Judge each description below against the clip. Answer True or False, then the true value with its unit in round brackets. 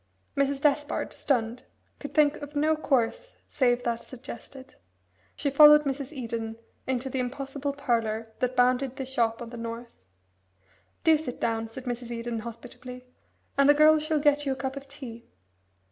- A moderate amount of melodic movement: True (3.3 semitones)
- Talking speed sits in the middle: True (160 wpm)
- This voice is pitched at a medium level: False (260 Hz)